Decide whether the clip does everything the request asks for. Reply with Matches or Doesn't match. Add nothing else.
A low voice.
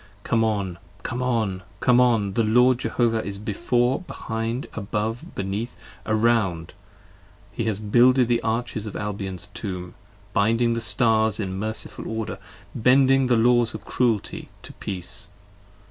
Matches